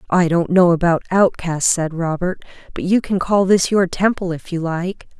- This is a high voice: No, medium, 175 Hz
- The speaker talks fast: No, average, 195 wpm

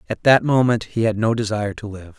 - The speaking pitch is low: Yes, low, 110 Hz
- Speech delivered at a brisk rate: Yes, fast, 245 wpm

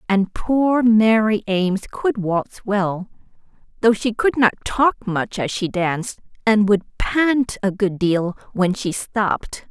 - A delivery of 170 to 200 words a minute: No, average, 155 wpm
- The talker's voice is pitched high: Yes, high, 210 Hz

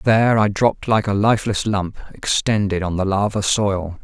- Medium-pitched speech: No, low, 100 Hz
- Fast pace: No, average, 180 wpm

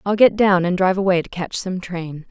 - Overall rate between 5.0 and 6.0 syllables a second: Yes, 5.5 syllables/s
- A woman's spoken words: Yes, female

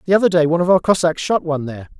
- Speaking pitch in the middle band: Yes, medium, 165 Hz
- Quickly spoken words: Yes, fast, 300 wpm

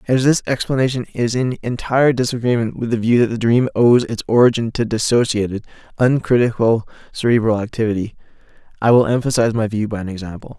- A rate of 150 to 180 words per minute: Yes, average, 165 wpm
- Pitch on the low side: Yes, low, 115 Hz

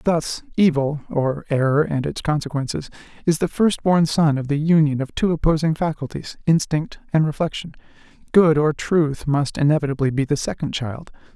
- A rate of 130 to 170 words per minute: Yes, average, 150 wpm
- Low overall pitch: No, medium, 150 Hz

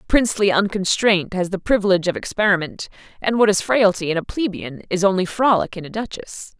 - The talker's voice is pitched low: No, high, 195 Hz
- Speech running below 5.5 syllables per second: No, 5.8 syllables/s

